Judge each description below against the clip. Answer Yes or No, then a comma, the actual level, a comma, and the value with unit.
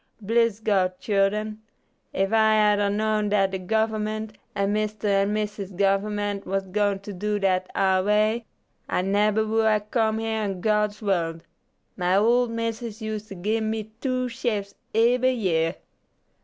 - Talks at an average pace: Yes, average, 155 wpm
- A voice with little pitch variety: Yes, narrow, 1.8 semitones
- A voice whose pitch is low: No, high, 210 Hz